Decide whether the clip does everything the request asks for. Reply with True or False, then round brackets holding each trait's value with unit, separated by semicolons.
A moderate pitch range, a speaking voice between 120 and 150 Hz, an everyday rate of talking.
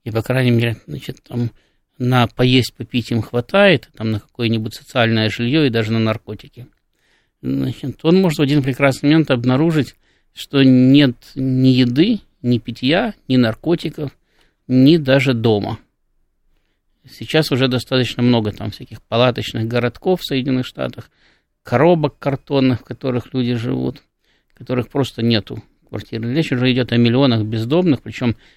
True (3.4 semitones; 125 Hz; 145 wpm)